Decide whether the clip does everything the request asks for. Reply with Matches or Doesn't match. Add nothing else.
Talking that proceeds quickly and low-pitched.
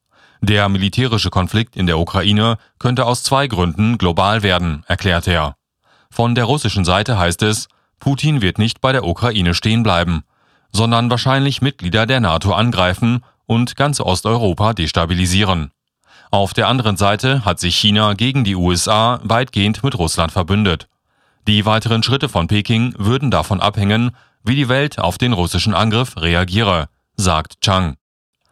Doesn't match